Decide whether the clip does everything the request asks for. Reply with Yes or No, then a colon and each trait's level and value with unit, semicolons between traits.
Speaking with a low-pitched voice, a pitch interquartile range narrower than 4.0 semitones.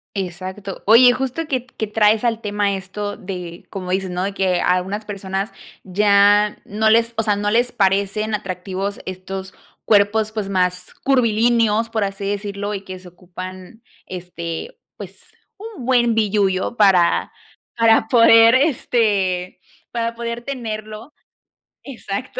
No: high, 205 Hz; average, 3.2 semitones